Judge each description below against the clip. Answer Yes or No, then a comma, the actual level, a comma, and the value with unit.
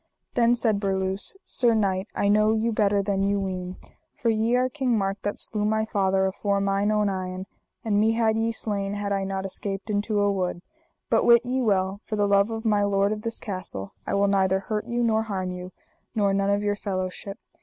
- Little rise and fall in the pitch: Yes, narrow, 2.1 semitones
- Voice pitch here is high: Yes, high, 205 Hz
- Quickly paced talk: Yes, fast, 215 wpm